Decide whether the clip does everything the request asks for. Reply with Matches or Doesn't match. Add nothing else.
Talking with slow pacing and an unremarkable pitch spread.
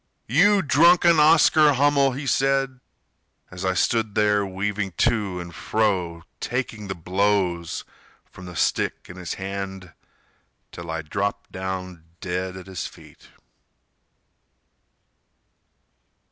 Doesn't match